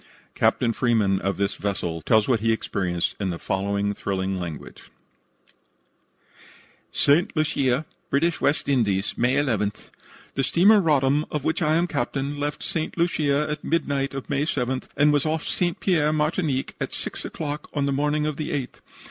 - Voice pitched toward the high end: No, medium, 140 Hz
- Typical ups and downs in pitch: No, wide, 5.7 semitones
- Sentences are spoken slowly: No, average, 165 wpm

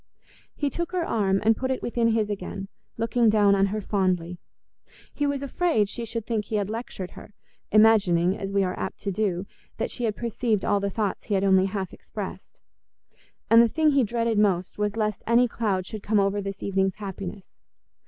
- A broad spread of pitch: No, average, 2.9 semitones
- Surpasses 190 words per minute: Yes, average, 200 wpm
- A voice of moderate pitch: No, high, 210 Hz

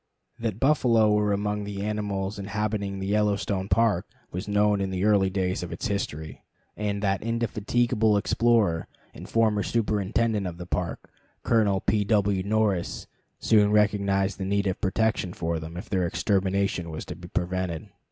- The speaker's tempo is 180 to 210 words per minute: No, average, 160 wpm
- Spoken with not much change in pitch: Yes, narrow, 2.0 semitones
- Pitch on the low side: Yes, low, 100 Hz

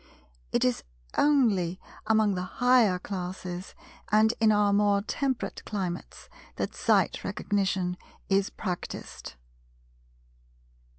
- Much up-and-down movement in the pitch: No, average, 3.1 semitones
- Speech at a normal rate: No, slow, 100 wpm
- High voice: Yes, high, 200 Hz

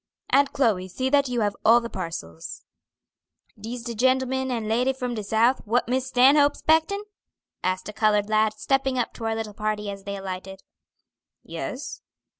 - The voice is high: Yes, high, 230 Hz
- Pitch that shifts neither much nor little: Yes, average, 4.0 semitones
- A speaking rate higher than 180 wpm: No, average, 170 wpm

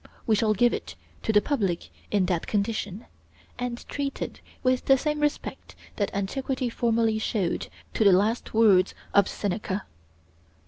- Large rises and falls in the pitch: No, average, 3.7 semitones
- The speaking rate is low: No, average, 150 wpm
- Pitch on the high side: Yes, high, 220 Hz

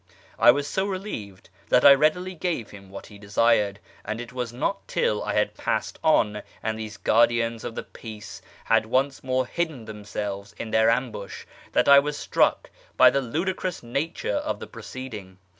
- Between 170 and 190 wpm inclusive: Yes, average, 175 wpm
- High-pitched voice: No, low, 120 Hz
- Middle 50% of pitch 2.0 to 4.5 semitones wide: No, average, 5.1 semitones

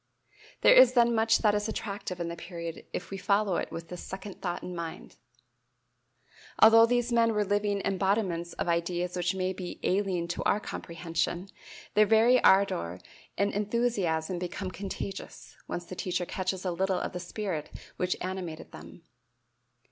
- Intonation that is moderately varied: Yes, average, 3.0 semitones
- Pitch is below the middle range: No, high, 190 Hz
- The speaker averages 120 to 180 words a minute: Yes, average, 165 wpm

